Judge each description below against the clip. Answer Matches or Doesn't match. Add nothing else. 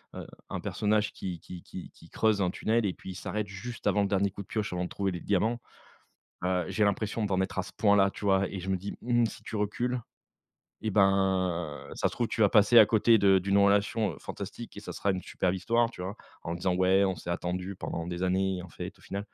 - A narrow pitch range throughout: Matches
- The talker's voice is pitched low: Matches